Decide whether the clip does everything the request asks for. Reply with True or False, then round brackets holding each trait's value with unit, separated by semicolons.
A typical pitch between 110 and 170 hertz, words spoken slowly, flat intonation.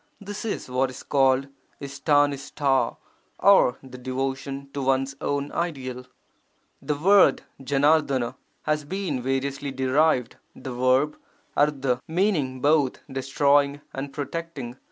True (140 Hz; 115 wpm; 2.1 semitones)